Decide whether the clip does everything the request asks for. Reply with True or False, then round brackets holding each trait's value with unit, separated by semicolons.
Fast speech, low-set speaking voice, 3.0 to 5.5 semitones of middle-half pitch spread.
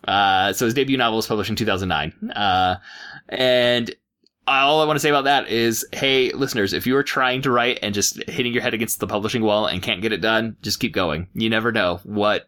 True (225 wpm; 115 Hz; 3.3 semitones)